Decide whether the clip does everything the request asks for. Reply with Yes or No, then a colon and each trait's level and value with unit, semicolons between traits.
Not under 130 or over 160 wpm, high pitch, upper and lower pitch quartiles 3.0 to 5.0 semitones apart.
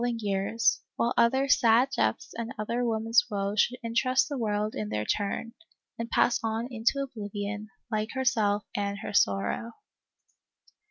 No: average, 150 wpm; high, 220 Hz; narrow, 2.5 semitones